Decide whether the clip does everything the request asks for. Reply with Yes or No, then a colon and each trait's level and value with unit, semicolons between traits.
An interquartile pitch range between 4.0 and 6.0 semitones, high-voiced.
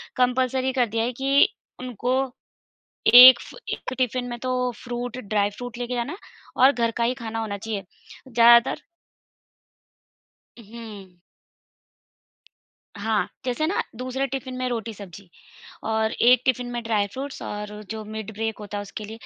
No: average, 2.8 semitones; high, 235 Hz